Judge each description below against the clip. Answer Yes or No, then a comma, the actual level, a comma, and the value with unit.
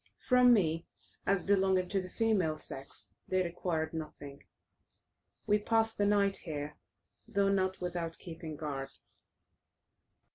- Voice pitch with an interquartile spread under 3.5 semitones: No, average, 4.1 semitones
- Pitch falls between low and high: Yes, medium, 180 Hz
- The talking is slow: Yes, slow, 120 wpm